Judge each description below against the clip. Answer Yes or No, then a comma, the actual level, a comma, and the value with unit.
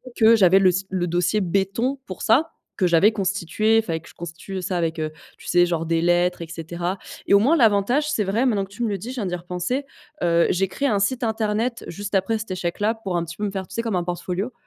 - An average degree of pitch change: Yes, average, 4.0 semitones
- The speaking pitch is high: Yes, high, 195 Hz